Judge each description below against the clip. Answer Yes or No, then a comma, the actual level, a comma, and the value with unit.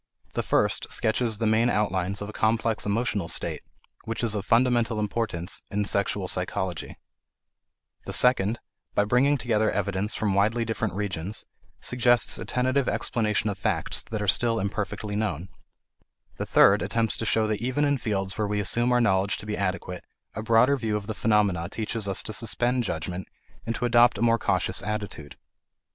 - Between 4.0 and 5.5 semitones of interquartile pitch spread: No, average, 2.7 semitones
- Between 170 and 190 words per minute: Yes, average, 175 wpm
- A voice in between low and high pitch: No, low, 110 Hz